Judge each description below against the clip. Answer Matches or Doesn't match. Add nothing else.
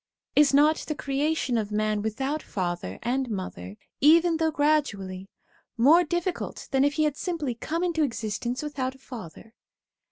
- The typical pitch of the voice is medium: Doesn't match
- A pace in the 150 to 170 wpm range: Matches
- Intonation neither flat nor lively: Doesn't match